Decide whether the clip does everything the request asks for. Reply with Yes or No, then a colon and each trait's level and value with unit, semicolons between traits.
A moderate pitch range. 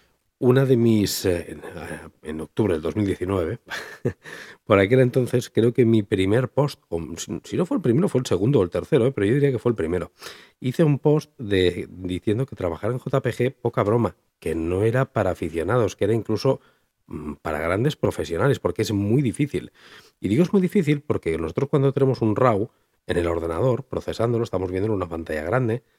No: wide, 6.3 semitones